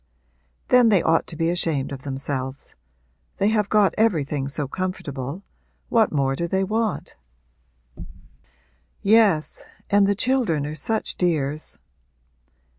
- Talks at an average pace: No, slow, 120 wpm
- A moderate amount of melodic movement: No, wide, 6.5 semitones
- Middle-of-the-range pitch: Yes, medium, 170 Hz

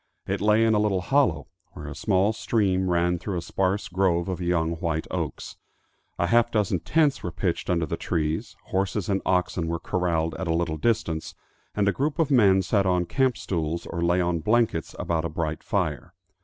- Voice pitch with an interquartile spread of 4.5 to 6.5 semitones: No, average, 3.7 semitones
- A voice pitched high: No, very low, 90 Hz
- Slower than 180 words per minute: No, average, 195 wpm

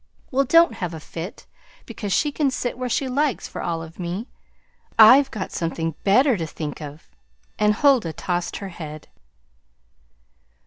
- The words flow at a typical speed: Yes, average, 155 wpm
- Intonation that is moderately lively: No, wide, 7.7 semitones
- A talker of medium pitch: No, high, 200 Hz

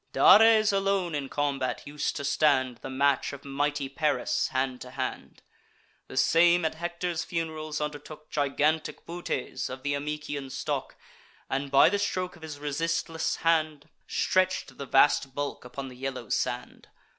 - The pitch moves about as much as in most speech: Yes, average, 3.3 semitones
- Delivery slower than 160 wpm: Yes, average, 150 wpm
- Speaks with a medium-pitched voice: Yes, medium, 145 Hz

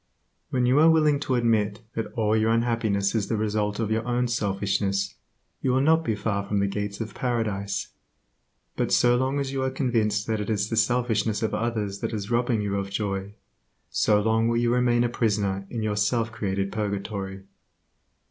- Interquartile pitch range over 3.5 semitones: No, average, 2.8 semitones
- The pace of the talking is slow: No, average, 195 wpm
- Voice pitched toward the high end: No, low, 110 Hz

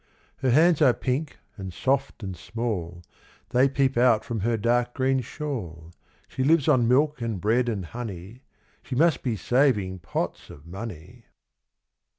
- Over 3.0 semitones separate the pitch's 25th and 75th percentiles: Yes, average, 5.3 semitones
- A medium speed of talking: Yes, average, 155 wpm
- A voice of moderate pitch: No, low, 120 Hz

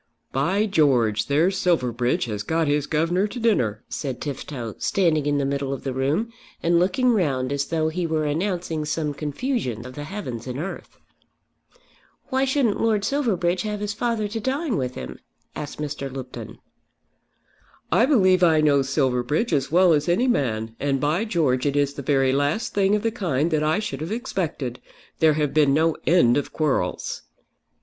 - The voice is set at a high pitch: No, medium, 155 Hz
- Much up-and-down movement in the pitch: Yes, wide, 6.1 semitones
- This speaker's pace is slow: No, average, 175 wpm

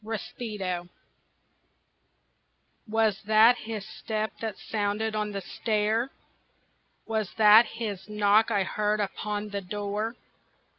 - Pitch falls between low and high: No, high, 210 Hz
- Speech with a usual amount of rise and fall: No, narrow, 1.4 semitones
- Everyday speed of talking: No, slow, 105 wpm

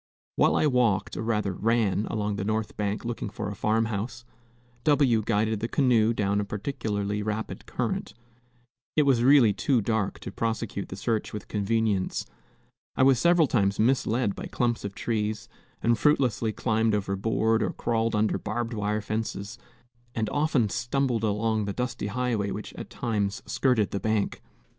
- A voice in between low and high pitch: No, low, 110 Hz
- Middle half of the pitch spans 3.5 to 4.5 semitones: No, narrow, 2.4 semitones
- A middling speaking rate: Yes, average, 165 wpm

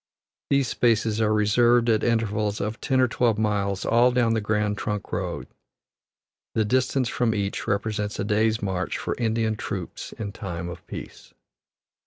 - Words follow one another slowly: No, average, 160 wpm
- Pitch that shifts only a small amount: Yes, narrow, 2.1 semitones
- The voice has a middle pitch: No, low, 110 Hz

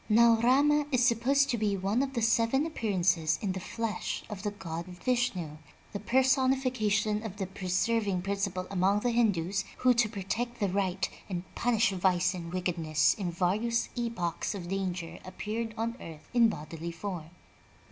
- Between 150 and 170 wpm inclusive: Yes, average, 160 wpm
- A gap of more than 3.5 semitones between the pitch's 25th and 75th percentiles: Yes, average, 4.4 semitones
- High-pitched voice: Yes, high, 205 Hz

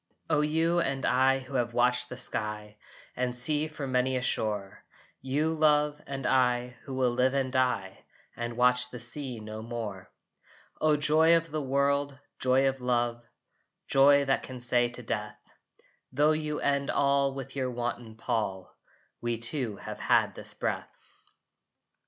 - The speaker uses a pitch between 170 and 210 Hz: No, low, 130 Hz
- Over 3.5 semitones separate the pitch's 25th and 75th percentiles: No, average, 2.8 semitones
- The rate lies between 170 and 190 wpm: No, average, 160 wpm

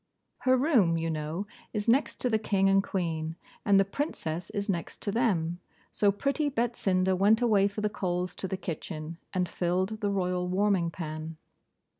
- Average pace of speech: Yes, average, 175 wpm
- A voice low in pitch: No, high, 190 Hz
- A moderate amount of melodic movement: Yes, average, 3.6 semitones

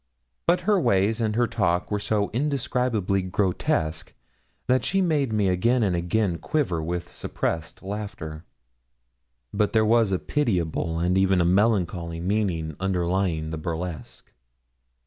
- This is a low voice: Yes, very low, 95 Hz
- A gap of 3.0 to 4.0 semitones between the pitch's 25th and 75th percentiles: No, average, 4.5 semitones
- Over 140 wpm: No, slow, 135 wpm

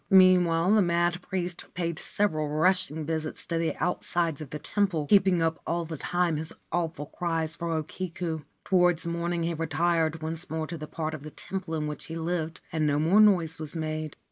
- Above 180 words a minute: Yes, average, 195 wpm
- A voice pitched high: No, medium, 165 Hz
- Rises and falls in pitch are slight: Yes, narrow, 2.0 semitones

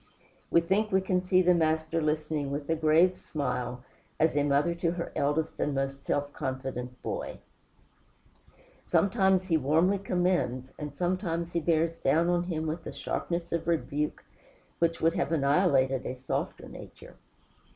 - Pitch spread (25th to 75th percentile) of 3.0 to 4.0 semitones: Yes, average, 3.6 semitones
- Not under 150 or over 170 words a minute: Yes, average, 155 wpm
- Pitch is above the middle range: No, medium, 160 Hz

